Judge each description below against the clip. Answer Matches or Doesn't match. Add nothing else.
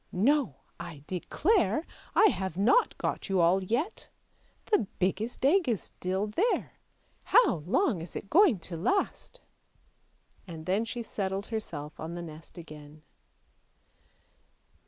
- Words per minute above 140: Doesn't match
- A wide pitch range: Matches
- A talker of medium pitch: Doesn't match